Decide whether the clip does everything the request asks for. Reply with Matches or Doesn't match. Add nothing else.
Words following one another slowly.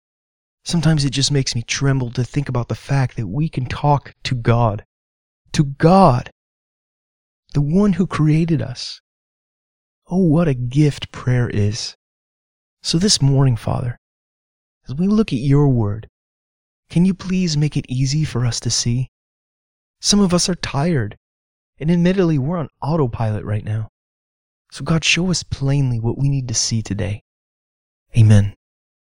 Doesn't match